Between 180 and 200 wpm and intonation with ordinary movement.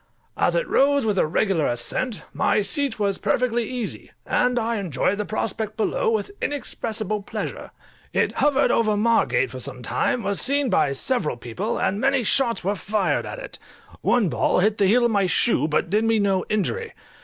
Yes: average, 185 wpm; average, 4.0 semitones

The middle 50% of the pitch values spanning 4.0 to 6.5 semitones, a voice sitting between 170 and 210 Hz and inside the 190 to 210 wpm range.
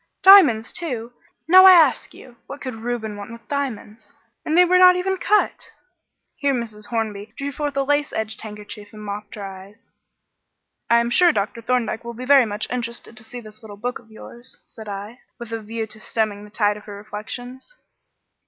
No: average, 4.4 semitones; high, 230 Hz; average, 195 wpm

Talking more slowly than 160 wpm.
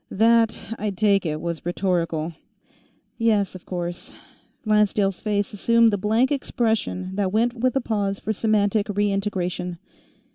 Yes: average, 140 wpm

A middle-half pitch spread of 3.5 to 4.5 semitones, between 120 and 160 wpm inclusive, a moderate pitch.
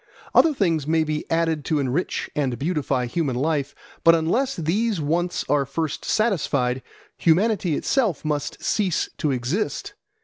Yes: average, 4.1 semitones; average, 140 wpm; medium, 160 Hz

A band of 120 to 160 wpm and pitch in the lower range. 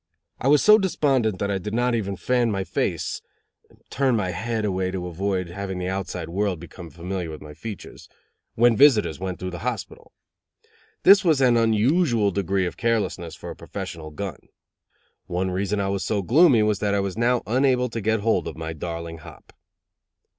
No: average, 185 wpm; low, 100 Hz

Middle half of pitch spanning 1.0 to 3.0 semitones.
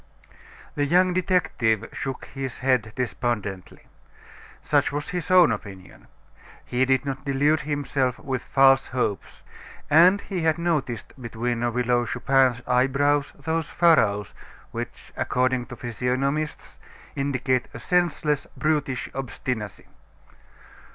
No: average, 3.5 semitones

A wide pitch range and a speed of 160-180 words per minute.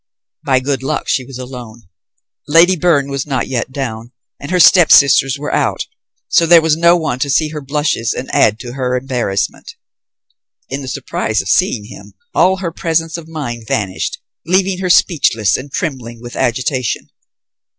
No: average, 4.7 semitones; average, 170 wpm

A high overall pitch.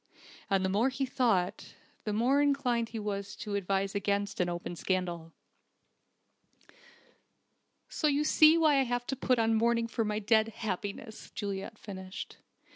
Yes: high, 215 Hz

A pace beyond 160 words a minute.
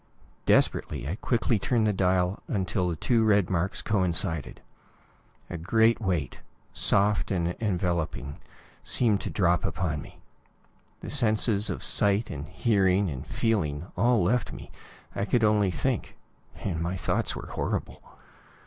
No: average, 140 wpm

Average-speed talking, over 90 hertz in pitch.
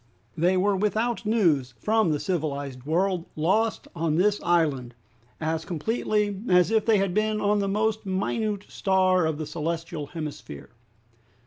Yes: average, 145 wpm; medium, 185 Hz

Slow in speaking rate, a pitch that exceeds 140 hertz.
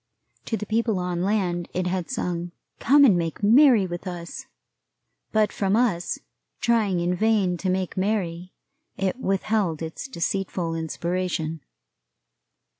Yes: slow, 130 wpm; medium, 185 Hz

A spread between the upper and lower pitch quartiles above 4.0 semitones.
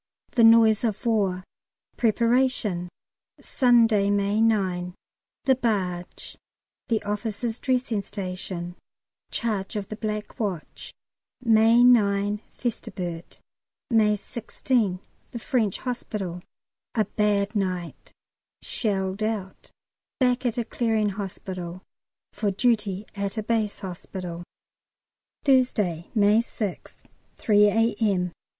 No: average, 3.2 semitones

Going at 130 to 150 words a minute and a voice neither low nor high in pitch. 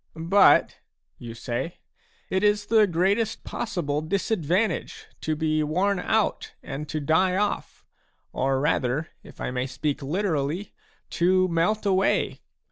Yes: average, 145 wpm; medium, 170 Hz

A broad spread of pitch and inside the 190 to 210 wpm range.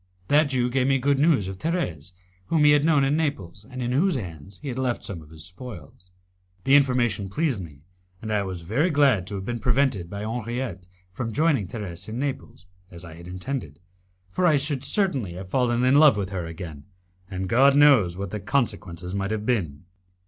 Yes: wide, 7.0 semitones; fast, 205 wpm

